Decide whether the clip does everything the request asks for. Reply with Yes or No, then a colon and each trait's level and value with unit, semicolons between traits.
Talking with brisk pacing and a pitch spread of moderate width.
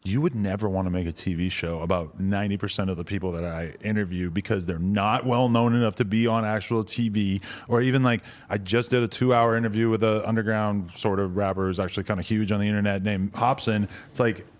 Yes: fast, 230 wpm; average, 3.1 semitones